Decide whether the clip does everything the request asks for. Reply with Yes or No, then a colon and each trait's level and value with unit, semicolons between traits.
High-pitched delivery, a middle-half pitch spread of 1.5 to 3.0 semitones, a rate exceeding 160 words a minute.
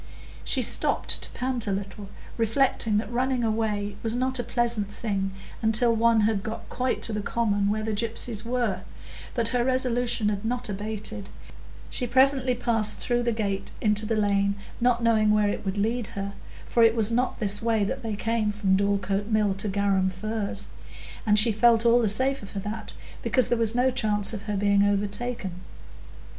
Yes: high, 220 Hz; average, 2.7 semitones; average, 185 wpm